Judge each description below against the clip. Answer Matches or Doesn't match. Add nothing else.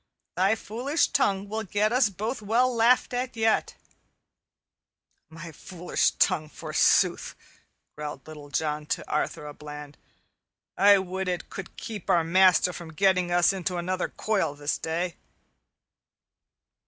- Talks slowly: Matches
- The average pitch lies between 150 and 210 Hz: Matches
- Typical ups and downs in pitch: Matches